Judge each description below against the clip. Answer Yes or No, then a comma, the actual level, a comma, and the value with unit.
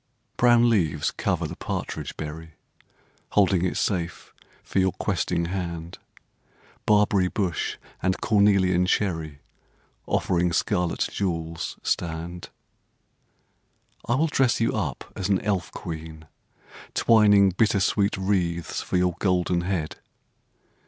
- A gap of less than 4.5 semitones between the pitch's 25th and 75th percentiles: Yes, average, 3.2 semitones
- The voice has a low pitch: Yes, very low, 90 Hz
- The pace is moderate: No, slow, 110 wpm